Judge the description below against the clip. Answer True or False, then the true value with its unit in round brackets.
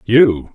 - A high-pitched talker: False (110 Hz)